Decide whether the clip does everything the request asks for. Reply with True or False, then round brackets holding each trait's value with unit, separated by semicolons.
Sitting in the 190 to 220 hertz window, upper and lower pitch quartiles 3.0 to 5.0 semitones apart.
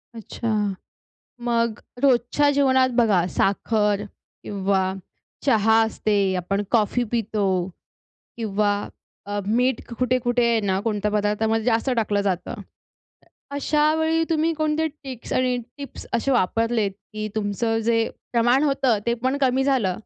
False (230 Hz; 3.9 semitones)